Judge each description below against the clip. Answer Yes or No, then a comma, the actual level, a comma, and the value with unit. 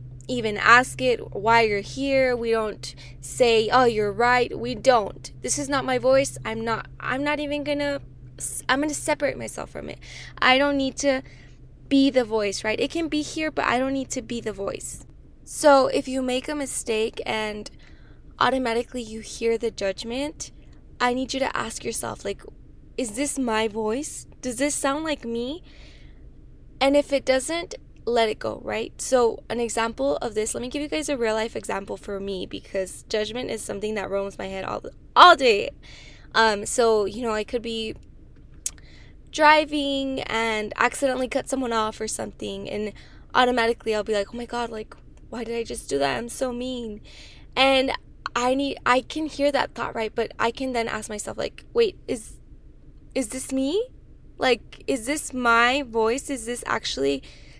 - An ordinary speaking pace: Yes, average, 185 wpm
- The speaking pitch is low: No, high, 245 Hz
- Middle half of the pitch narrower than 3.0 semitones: No, average, 3.8 semitones